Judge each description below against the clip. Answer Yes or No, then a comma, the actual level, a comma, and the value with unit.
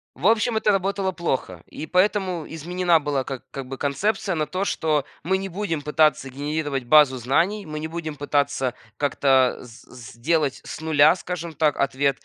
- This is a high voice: No, medium, 155 Hz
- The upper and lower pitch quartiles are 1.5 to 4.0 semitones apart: No, average, 4.6 semitones